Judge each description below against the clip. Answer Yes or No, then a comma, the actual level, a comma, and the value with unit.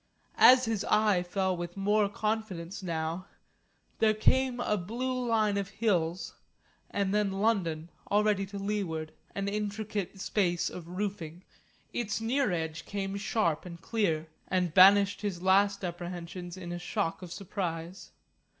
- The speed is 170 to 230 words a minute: No, average, 140 wpm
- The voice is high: Yes, high, 195 Hz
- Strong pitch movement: No, average, 3.2 semitones